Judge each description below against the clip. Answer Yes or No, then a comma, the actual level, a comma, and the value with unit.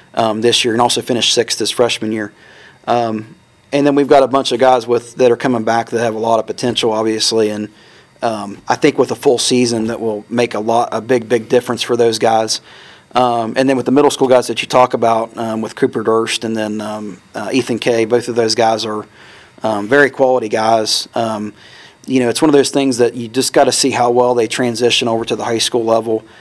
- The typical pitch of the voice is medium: No, low, 115 Hz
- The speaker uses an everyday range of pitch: No, narrow, 1.9 semitones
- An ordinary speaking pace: No, fast, 240 wpm